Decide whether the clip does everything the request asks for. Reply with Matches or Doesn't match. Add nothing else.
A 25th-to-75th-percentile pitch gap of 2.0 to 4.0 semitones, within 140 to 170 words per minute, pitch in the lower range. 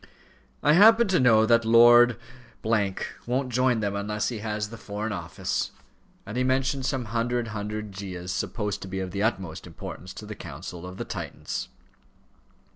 Matches